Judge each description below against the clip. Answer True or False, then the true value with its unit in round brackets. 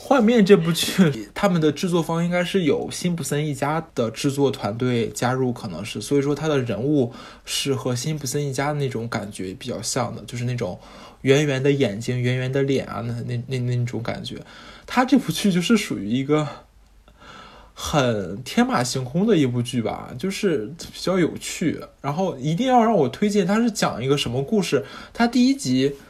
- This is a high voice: False (140 Hz)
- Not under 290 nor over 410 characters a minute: False (280 characters per minute)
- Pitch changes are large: True (6.5 semitones)